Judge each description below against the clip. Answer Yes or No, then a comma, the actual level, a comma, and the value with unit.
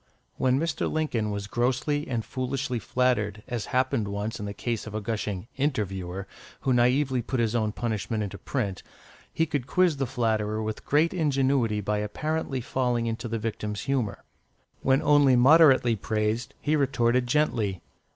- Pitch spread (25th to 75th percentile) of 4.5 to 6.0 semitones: No, average, 4.1 semitones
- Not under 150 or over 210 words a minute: Yes, average, 160 wpm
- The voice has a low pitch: Yes, low, 120 Hz